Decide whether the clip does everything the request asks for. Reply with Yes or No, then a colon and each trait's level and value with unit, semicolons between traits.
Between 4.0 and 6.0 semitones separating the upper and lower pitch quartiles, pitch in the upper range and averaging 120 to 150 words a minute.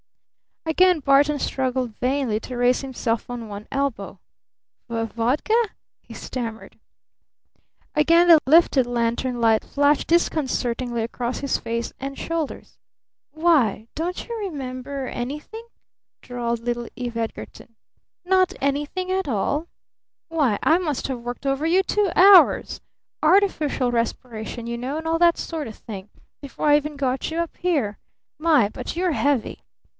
Yes: average, 5.3 semitones; very high, 275 Hz; slow, 135 wpm